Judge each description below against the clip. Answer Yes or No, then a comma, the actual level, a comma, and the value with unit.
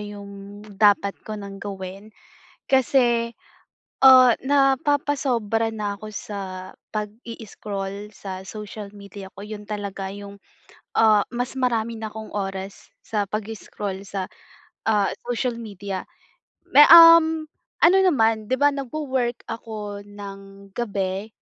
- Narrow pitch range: No, average, 3.2 semitones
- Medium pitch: No, high, 210 Hz